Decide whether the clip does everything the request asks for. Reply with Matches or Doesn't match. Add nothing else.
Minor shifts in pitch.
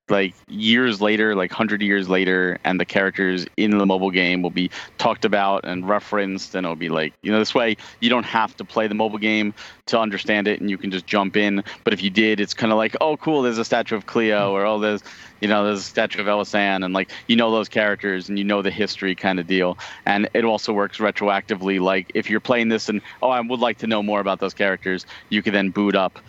Matches